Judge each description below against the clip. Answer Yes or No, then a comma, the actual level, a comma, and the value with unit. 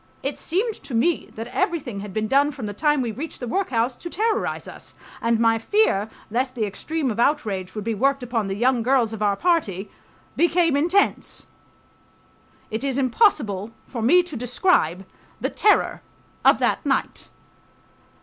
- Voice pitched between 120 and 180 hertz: No, very high, 250 Hz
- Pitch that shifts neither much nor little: No, wide, 6.5 semitones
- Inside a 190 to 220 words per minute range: No, average, 170 wpm